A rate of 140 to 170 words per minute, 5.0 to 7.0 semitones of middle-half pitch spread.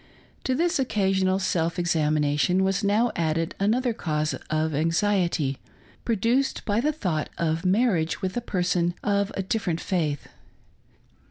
No: average, 145 wpm; average, 4.6 semitones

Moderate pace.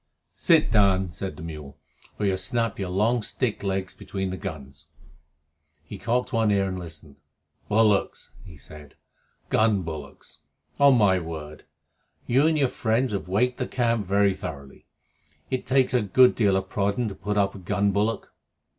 Yes: average, 165 wpm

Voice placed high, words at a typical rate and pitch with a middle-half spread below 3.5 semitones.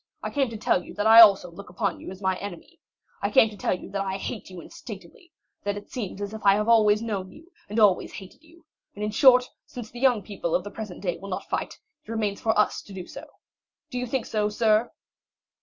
No: high, 210 Hz; fast, 245 wpm; average, 2.8 semitones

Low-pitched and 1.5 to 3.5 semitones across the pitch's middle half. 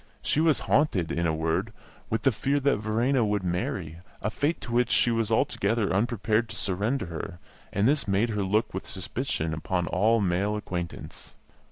No: low, 105 Hz; average, 4.4 semitones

